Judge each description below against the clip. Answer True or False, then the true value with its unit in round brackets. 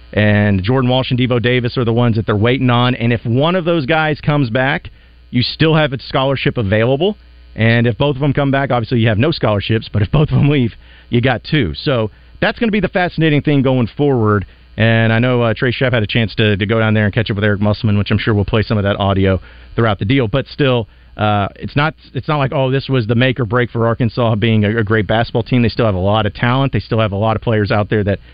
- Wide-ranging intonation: False (3.8 semitones)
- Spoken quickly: True (275 wpm)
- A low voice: True (120 Hz)